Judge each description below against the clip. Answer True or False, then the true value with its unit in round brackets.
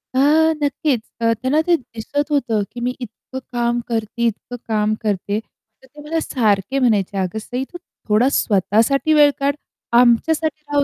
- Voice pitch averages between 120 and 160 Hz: False (245 Hz)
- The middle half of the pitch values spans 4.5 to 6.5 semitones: True (4.9 semitones)